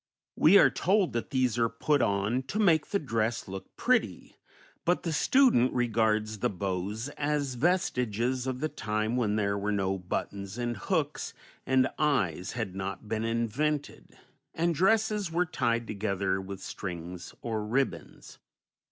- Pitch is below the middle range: Yes, low, 115 Hz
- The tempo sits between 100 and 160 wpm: Yes, average, 150 wpm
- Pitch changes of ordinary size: No, wide, 6.3 semitones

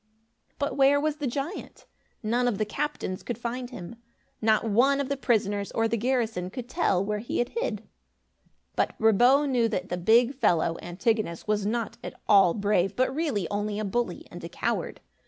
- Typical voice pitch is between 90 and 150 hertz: No, high, 230 Hz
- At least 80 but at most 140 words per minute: No, average, 185 wpm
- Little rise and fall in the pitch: No, average, 4.2 semitones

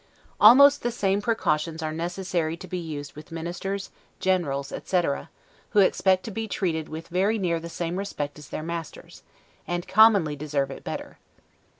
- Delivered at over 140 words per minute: Yes, average, 165 wpm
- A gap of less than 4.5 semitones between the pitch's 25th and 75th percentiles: Yes, average, 3.7 semitones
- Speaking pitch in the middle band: Yes, medium, 175 Hz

